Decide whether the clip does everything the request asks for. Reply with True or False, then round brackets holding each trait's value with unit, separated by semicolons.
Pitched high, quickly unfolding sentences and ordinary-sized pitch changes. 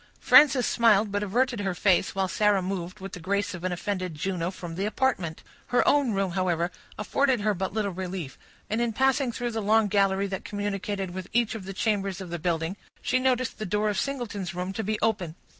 True (200 Hz; 210 wpm; 3.2 semitones)